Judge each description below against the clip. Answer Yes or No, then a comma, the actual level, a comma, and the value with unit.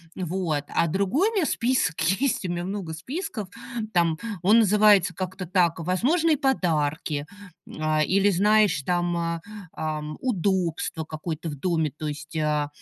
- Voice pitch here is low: No, medium, 175 Hz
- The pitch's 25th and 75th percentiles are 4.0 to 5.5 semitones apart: Yes, average, 4.5 semitones